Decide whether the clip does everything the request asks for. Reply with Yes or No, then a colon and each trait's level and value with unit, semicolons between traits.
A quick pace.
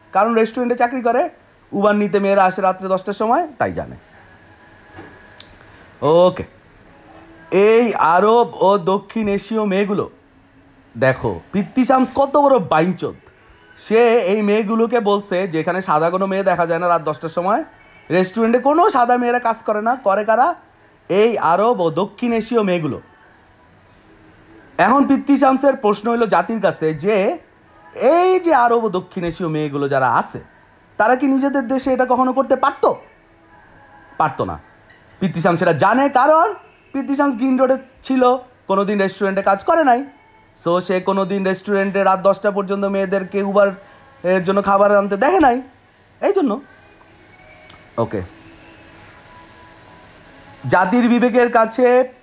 Yes: fast, 130 wpm